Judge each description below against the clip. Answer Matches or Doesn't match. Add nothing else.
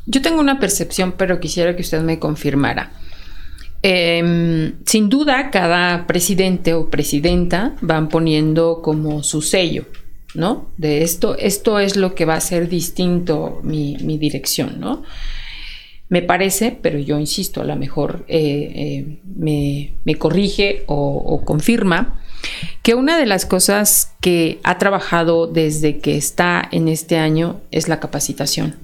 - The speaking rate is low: Doesn't match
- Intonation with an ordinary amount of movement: Matches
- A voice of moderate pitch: Matches